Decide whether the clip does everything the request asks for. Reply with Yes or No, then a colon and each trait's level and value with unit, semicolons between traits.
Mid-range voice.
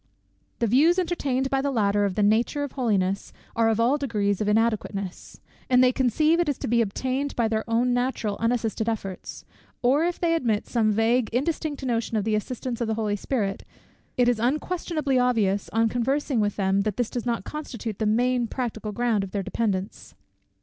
No: high, 235 Hz